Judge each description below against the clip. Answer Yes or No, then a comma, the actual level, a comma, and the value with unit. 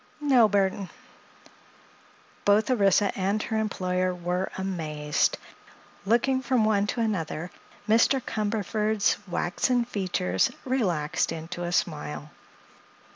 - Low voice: No, high, 195 Hz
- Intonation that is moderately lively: Yes, average, 3.8 semitones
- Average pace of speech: No, slow, 100 wpm